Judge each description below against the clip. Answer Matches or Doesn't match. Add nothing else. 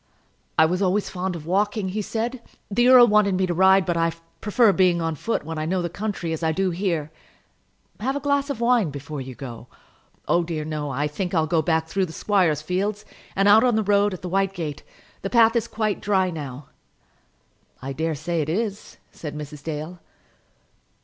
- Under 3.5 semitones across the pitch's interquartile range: Doesn't match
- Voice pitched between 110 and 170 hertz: Doesn't match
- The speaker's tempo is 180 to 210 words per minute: Matches